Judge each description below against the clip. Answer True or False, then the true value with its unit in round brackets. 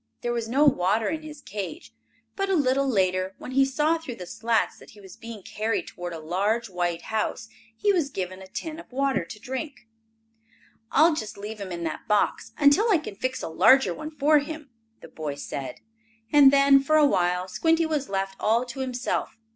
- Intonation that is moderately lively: False (7.1 semitones)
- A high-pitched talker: True (240 Hz)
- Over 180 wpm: True (200 wpm)